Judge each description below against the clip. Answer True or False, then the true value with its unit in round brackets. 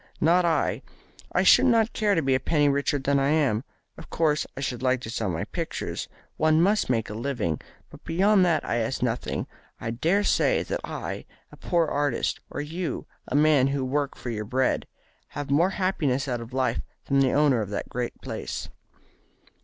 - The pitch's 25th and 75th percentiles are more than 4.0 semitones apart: True (4.5 semitones)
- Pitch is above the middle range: False (140 Hz)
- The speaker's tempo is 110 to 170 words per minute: False (195 wpm)